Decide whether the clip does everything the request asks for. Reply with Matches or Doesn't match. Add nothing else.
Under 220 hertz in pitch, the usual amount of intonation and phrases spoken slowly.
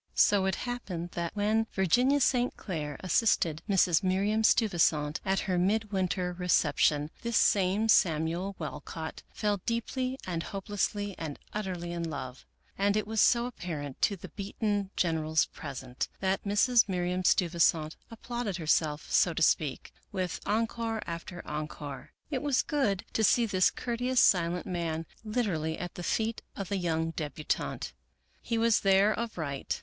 Doesn't match